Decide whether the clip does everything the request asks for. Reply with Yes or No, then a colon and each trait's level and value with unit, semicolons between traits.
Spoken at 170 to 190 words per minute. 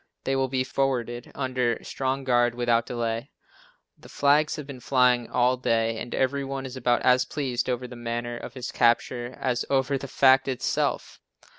Yes: average, 175 wpm